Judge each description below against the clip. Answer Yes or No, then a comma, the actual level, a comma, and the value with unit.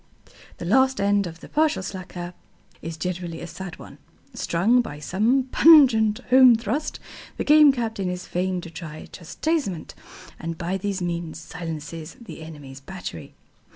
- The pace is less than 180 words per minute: Yes, average, 150 wpm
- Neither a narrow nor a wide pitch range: No, wide, 5.7 semitones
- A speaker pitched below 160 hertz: No, medium, 185 Hz